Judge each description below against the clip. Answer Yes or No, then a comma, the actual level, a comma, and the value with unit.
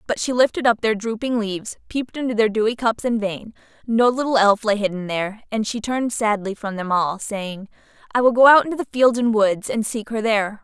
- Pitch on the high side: Yes, high, 220 Hz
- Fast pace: Yes, fast, 230 wpm